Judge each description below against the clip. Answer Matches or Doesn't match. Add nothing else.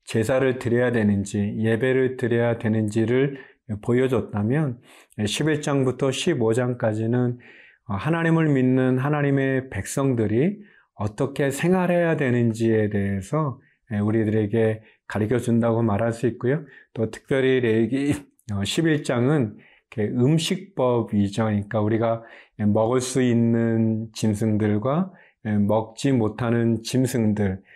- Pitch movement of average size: Matches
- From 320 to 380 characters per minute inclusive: Doesn't match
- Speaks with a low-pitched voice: Matches